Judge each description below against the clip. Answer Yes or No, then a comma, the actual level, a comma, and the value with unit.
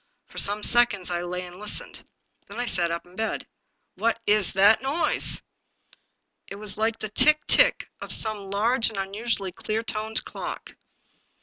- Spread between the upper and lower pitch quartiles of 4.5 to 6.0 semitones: No, average, 2.8 semitones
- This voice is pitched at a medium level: No, high, 210 Hz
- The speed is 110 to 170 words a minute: Yes, average, 165 wpm